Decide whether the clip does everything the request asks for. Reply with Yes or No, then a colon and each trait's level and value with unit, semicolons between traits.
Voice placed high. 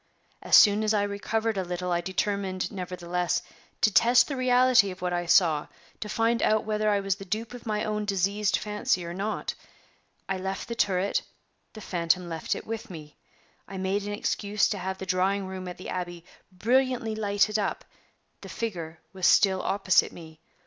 Yes: high, 195 Hz